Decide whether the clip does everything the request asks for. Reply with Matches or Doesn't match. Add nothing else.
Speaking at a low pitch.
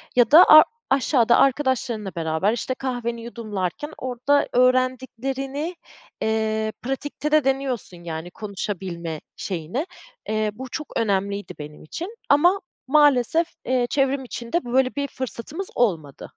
Doesn't match